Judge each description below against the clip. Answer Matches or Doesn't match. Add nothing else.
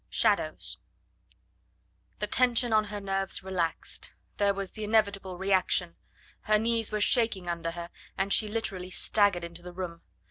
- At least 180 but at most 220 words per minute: Doesn't match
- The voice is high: Matches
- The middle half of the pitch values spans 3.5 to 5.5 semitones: Doesn't match